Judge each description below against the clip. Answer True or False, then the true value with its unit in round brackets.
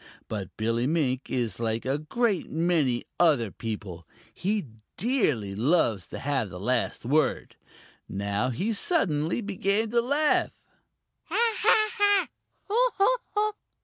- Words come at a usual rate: False (115 wpm)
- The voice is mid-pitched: True (150 Hz)